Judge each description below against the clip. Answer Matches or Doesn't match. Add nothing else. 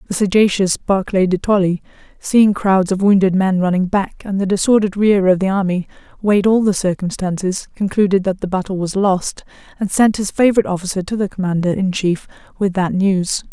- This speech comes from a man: Doesn't match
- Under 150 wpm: Doesn't match